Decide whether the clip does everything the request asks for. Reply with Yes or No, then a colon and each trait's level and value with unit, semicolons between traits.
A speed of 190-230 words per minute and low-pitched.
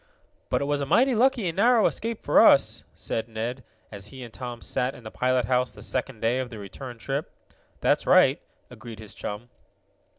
Yes: average, 200 wpm; low, 125 Hz